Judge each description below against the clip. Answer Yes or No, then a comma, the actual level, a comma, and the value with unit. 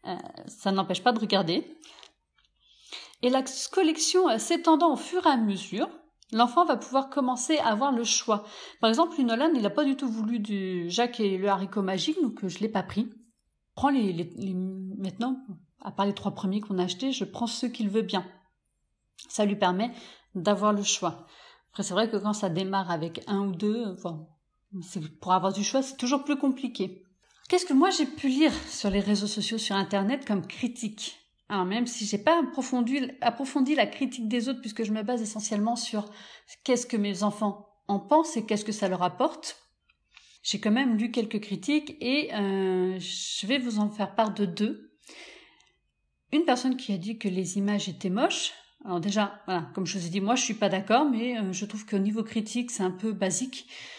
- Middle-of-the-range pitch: No, high, 215 Hz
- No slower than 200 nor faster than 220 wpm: Yes, average, 205 wpm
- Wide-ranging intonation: No, average, 4.9 semitones